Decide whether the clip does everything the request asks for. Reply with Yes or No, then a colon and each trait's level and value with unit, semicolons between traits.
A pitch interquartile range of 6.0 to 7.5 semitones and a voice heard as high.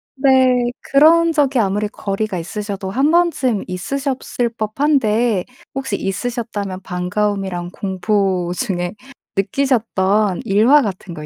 No: wide, 5.4 semitones; high, 210 Hz